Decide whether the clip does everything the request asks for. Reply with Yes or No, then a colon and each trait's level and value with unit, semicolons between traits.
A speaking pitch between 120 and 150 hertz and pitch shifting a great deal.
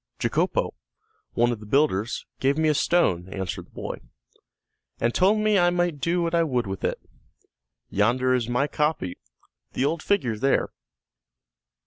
Yes: low, 135 Hz; wide, 6.5 semitones